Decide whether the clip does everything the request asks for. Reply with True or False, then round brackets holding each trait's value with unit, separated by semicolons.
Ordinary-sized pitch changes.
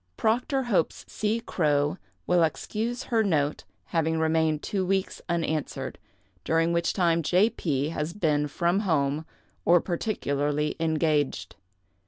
True (4.2 semitones)